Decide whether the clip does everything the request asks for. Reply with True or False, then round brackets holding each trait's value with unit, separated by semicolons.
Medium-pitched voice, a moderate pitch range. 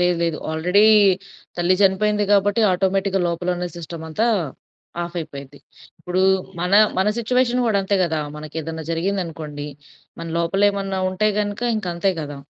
True (180 Hz; 3.5 semitones)